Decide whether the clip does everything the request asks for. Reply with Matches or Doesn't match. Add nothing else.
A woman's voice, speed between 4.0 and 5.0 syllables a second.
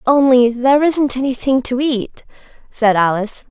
Matches